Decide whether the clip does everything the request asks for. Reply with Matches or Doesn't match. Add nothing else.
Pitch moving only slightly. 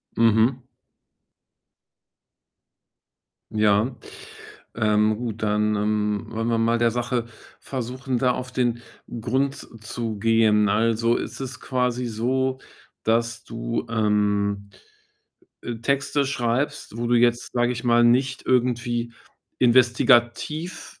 Matches